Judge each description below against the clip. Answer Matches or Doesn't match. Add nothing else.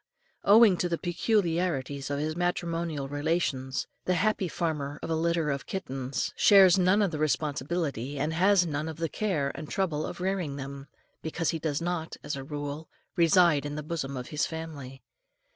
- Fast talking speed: Doesn't match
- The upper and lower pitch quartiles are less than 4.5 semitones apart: Matches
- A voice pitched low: Doesn't match